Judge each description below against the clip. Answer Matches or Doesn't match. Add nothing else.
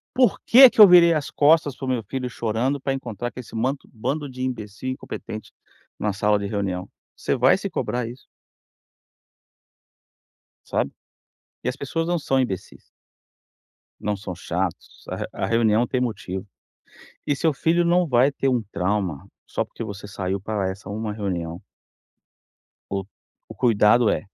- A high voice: Doesn't match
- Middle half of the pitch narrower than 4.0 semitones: Doesn't match